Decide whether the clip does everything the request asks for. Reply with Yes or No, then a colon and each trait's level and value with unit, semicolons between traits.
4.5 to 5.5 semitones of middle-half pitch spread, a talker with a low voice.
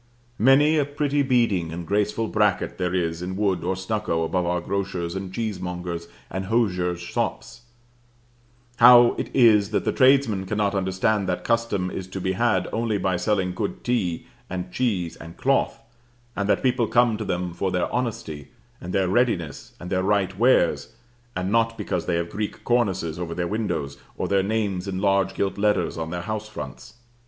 No: average, 4.0 semitones; very low, 95 Hz